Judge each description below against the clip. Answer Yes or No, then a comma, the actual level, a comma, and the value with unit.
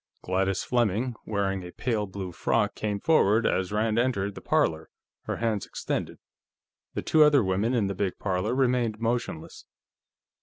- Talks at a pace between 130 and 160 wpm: Yes, average, 155 wpm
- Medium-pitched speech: No, low, 105 Hz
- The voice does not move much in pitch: No, average, 3.6 semitones